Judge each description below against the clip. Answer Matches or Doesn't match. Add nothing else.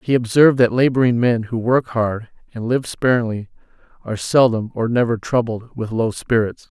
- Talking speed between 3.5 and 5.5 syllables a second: Matches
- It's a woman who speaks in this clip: Doesn't match